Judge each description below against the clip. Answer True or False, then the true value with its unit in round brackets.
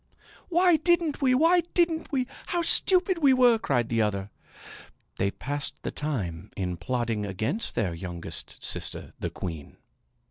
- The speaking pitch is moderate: True (145 Hz)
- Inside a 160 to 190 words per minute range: False (145 wpm)